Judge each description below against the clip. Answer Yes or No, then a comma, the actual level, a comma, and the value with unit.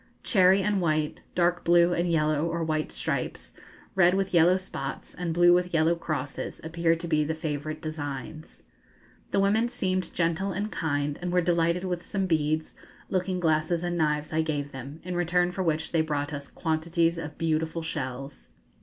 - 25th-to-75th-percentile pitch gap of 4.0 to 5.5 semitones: No, narrow, 2.4 semitones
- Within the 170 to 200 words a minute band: Yes, average, 175 wpm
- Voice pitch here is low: No, medium, 165 Hz